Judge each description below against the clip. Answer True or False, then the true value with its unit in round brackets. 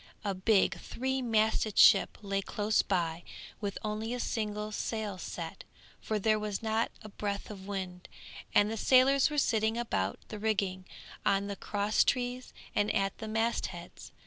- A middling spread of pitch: False (2.2 semitones)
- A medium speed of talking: True (165 wpm)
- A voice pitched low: False (210 Hz)